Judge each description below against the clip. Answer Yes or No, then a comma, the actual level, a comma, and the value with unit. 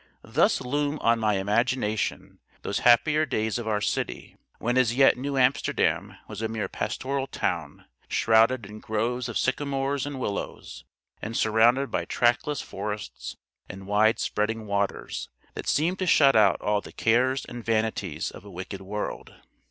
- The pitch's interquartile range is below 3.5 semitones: No, average, 3.9 semitones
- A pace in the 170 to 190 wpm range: No, average, 155 wpm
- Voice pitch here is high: No, low, 115 Hz